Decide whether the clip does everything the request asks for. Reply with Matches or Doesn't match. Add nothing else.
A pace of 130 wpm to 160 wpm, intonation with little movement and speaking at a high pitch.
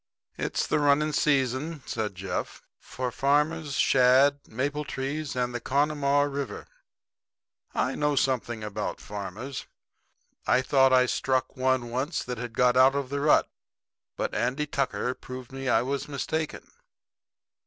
Doesn't match